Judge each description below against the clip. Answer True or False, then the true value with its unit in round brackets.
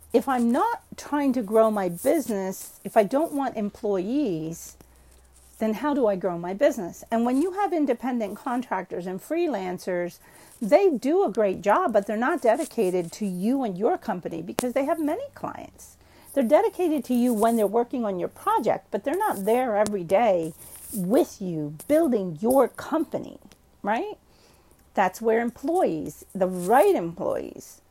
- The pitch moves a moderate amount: False (7.0 semitones)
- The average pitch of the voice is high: True (230 Hz)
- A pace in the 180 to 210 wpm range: False (160 wpm)